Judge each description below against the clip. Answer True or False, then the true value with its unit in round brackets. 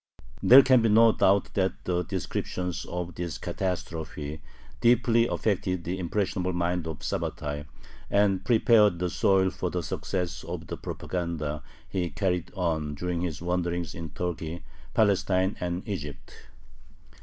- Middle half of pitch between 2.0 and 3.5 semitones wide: True (2.4 semitones)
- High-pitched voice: False (90 Hz)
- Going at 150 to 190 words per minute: False (135 wpm)